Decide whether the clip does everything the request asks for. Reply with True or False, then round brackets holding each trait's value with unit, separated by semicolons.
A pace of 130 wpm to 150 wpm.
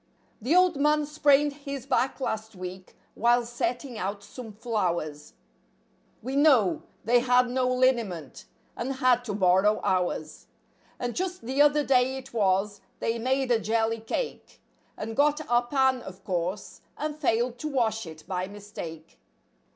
True (145 wpm)